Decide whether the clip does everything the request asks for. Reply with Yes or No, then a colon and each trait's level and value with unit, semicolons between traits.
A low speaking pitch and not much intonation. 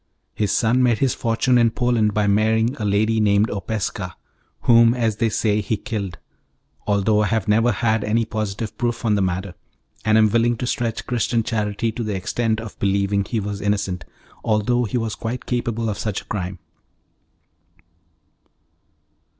Yes: low, 110 Hz; narrow, 2.2 semitones